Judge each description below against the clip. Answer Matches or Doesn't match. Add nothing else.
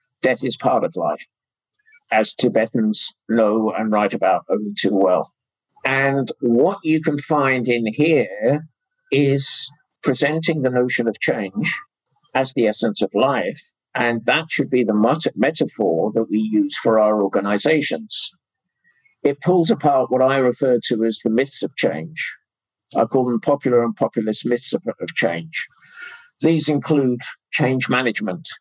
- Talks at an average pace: Matches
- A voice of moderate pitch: Doesn't match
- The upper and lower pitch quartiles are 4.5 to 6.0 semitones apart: Matches